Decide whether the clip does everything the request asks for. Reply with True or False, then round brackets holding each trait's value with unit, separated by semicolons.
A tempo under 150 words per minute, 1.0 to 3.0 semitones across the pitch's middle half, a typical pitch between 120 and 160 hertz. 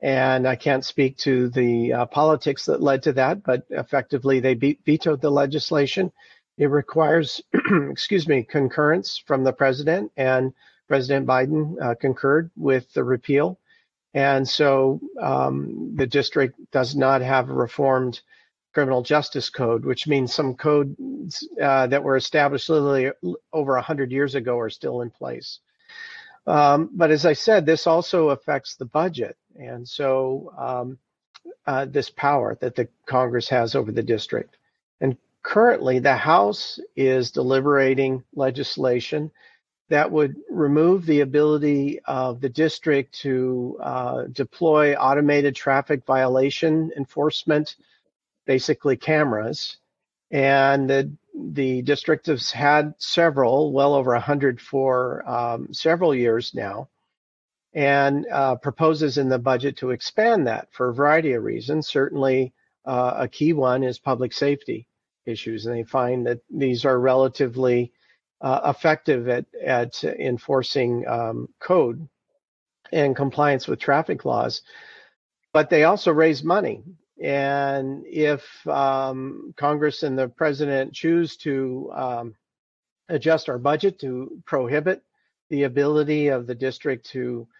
True (135 wpm; 2.7 semitones; 140 Hz)